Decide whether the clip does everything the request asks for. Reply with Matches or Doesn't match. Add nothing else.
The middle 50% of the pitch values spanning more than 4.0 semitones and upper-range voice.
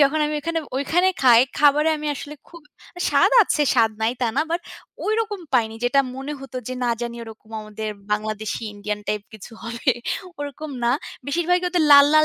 Matches